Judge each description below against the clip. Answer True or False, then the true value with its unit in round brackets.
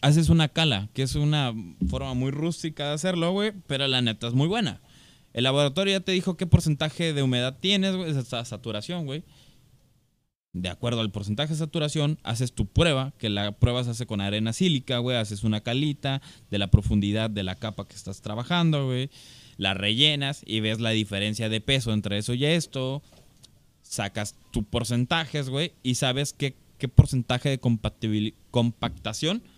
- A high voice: False (130 Hz)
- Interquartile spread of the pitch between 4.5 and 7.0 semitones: True (5.1 semitones)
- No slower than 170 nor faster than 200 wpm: True (175 wpm)